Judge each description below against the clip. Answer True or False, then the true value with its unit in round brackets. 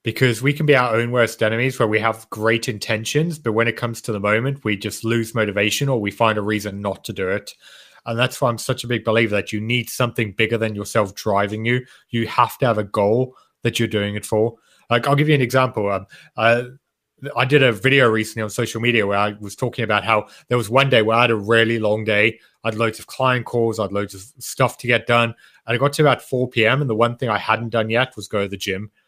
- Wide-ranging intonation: False (2.5 semitones)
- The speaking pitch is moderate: False (115 Hz)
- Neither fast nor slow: False (260 wpm)